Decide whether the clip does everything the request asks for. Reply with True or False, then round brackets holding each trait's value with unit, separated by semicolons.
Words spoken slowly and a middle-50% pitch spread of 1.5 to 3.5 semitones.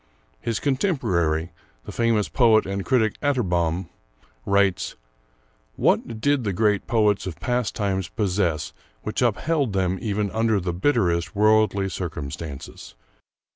False (120 wpm; 4.1 semitones)